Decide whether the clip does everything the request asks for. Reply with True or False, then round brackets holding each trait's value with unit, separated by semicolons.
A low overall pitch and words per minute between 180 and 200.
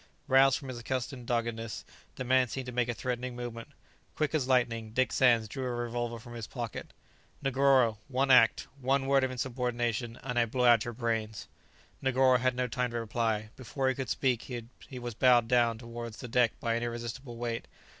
True (120 Hz; 195 wpm)